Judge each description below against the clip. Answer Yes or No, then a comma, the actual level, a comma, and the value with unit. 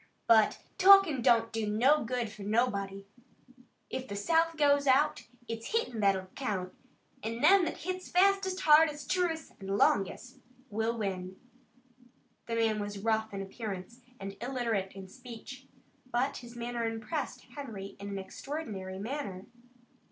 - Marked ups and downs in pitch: Yes, wide, 6.0 semitones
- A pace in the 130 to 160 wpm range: Yes, average, 140 wpm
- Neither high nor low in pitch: No, high, 230 Hz